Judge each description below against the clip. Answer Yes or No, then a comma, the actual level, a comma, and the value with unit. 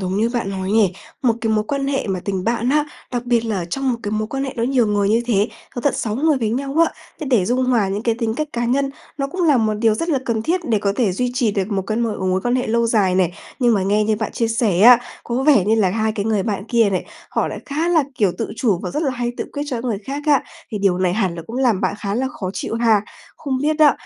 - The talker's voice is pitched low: No, high, 230 Hz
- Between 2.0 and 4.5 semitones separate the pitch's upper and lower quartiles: Yes, average, 4.0 semitones